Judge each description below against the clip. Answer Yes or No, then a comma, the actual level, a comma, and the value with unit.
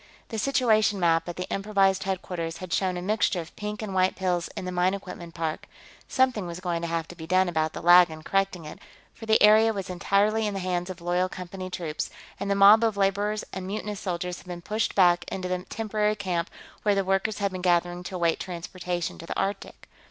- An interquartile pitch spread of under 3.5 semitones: Yes, narrow, 2.6 semitones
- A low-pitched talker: No, medium, 185 Hz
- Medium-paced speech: No, fast, 225 wpm